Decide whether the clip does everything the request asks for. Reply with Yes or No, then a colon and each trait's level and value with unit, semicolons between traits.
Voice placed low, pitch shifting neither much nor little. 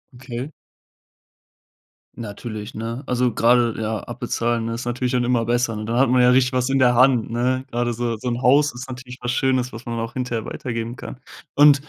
No: low, 120 Hz; narrow, 1.7 semitones